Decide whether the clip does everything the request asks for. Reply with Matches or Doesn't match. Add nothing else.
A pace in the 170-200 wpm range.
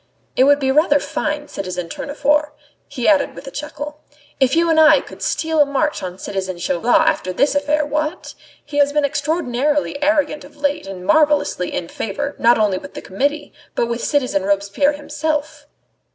Matches